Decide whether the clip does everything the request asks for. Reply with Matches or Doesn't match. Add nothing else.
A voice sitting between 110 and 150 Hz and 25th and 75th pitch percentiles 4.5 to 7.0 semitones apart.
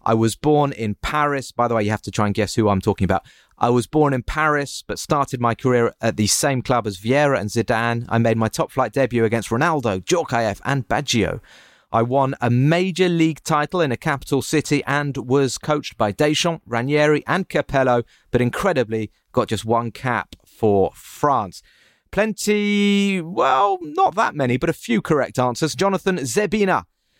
Matches